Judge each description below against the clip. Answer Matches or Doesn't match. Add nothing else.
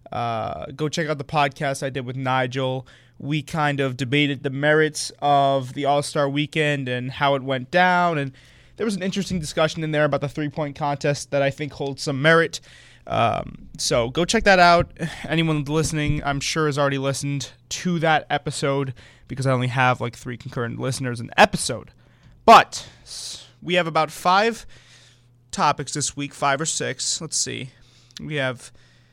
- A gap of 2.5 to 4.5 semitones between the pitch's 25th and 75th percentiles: Matches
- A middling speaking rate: Matches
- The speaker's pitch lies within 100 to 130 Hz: Doesn't match